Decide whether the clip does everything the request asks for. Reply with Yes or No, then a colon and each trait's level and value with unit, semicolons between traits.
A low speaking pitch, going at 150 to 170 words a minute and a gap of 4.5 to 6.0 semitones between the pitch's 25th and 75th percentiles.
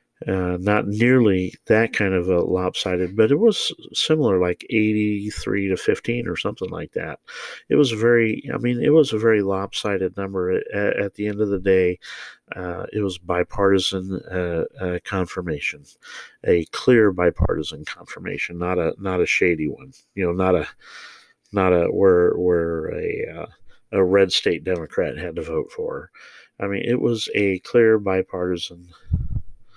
Yes: low, 105 Hz; average, 160 wpm; average, 5.1 semitones